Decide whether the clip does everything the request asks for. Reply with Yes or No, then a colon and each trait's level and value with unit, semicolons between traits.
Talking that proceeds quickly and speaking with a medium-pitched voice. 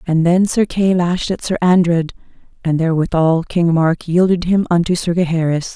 No: average, 175 wpm; medium, 170 Hz